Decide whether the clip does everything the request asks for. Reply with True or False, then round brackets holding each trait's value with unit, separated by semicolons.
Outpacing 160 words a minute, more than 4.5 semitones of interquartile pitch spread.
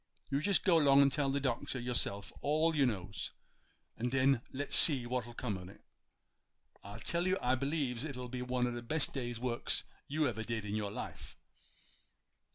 False (180 wpm; 3.2 semitones)